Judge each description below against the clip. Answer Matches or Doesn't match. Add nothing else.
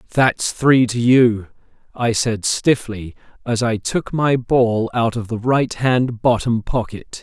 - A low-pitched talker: Matches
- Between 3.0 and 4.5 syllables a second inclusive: Matches